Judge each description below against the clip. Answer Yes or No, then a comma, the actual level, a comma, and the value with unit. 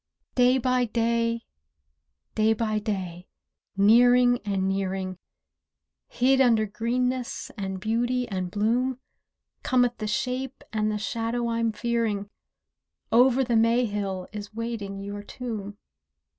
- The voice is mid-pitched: No, high, 230 Hz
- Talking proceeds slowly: Yes, slow, 115 wpm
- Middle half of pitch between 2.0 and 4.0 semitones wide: Yes, average, 3.1 semitones